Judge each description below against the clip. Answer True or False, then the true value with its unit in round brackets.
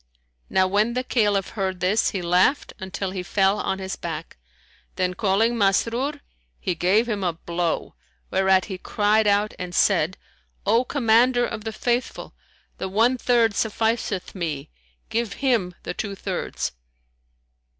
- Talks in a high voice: True (205 Hz)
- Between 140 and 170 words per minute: True (145 wpm)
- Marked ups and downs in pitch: False (3.5 semitones)